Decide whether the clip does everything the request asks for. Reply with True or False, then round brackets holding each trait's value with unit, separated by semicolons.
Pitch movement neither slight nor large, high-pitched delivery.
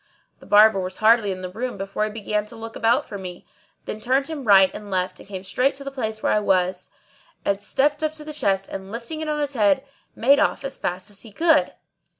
False (5.8 semitones; 215 Hz)